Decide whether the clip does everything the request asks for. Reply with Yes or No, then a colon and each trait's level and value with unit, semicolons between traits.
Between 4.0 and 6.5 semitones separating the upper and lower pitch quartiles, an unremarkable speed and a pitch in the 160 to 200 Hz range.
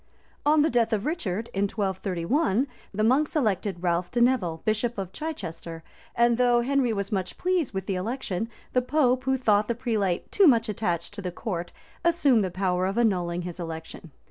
No: wide, 5.4 semitones; average, 185 wpm; high, 215 Hz